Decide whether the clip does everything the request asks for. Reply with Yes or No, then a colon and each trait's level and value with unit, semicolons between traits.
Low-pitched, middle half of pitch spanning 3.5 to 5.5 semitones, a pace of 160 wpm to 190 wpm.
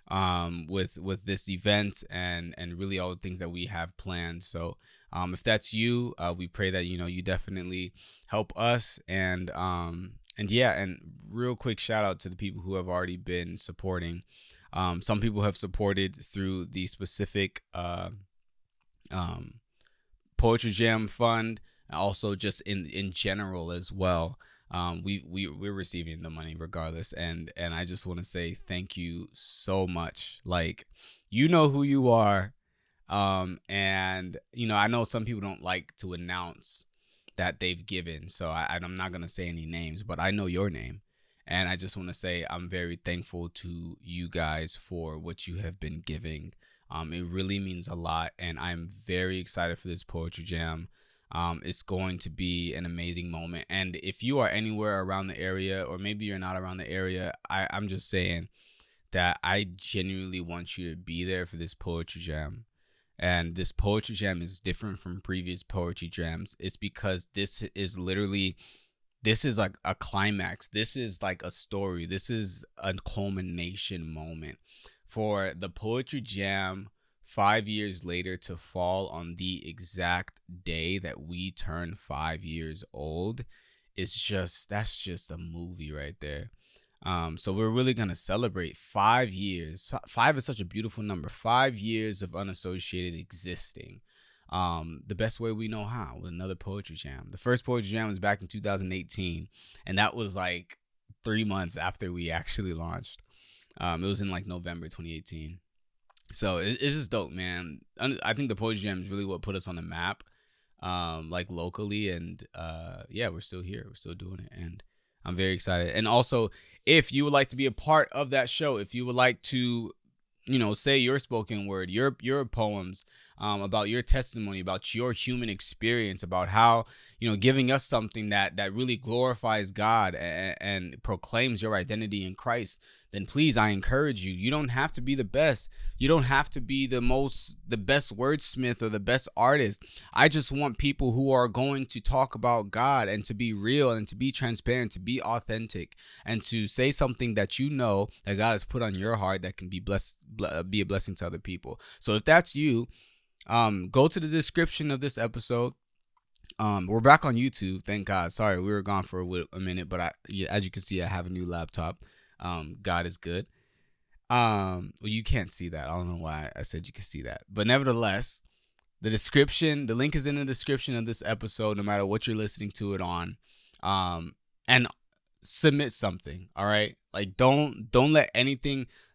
Yes: very low, 95 Hz; average, 4.0 semitones; average, 185 wpm